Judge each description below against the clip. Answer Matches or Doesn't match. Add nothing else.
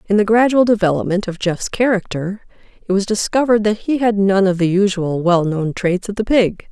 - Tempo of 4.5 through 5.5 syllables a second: Matches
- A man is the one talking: Doesn't match